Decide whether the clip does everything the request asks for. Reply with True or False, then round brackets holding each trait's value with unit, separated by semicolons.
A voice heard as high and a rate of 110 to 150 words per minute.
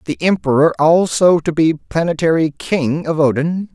False (160 Hz; 145 wpm)